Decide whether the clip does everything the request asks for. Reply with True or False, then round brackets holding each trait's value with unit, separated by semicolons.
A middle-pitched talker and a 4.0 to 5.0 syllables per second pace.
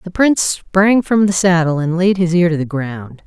True (180 Hz; 4.8 syllables/s)